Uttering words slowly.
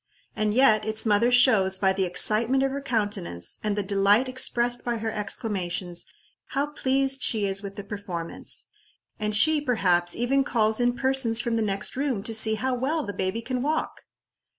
No: average, 180 wpm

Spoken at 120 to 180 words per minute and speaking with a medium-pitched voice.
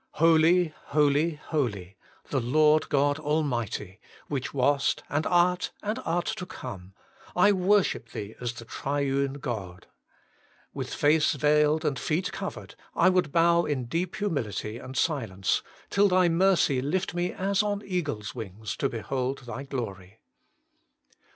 Yes: average, 140 wpm; medium, 145 Hz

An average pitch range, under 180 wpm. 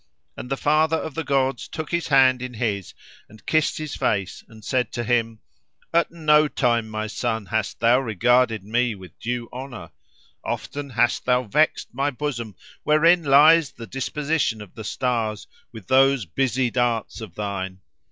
Yes: average, 4.2 semitones; average, 160 wpm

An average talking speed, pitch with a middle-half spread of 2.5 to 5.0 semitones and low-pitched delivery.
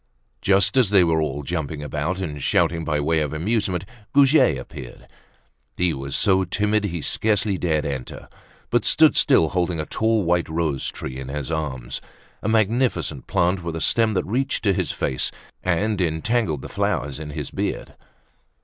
No: average, 170 wpm; wide, 5.4 semitones; very low, 85 Hz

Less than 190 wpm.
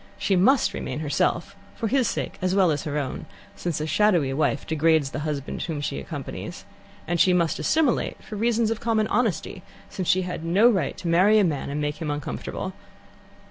No: average, 195 wpm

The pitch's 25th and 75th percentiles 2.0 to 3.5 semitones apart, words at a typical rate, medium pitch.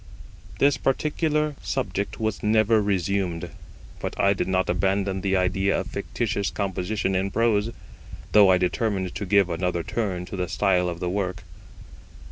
No: narrow, 2.5 semitones; average, 150 wpm; low, 100 Hz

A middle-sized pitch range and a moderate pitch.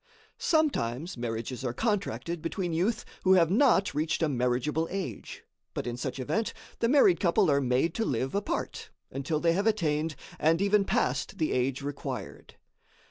No: wide, 7.0 semitones; medium, 160 Hz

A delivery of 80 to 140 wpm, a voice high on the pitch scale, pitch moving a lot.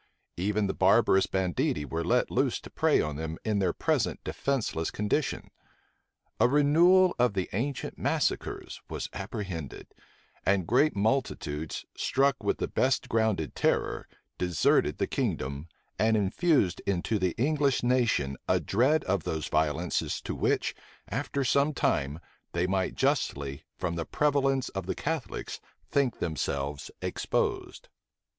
No: slow, 135 wpm; low, 100 Hz; wide, 8.3 semitones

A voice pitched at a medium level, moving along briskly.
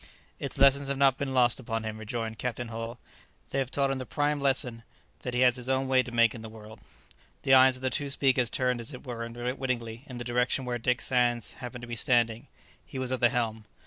No: low, 125 Hz; fast, 240 wpm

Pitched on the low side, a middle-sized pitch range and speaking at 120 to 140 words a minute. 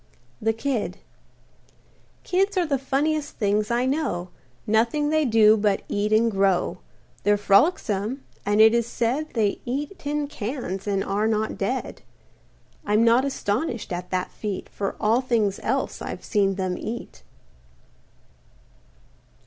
No: high, 220 Hz; average, 4.8 semitones; slow, 135 wpm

